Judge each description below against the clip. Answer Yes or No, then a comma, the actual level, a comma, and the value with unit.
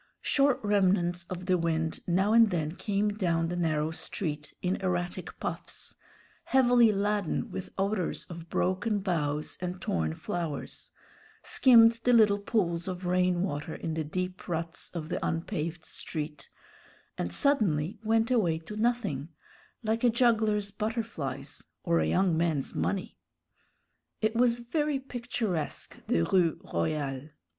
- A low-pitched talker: No, medium, 185 Hz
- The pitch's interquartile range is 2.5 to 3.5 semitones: No, average, 5.0 semitones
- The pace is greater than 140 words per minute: No, slow, 135 wpm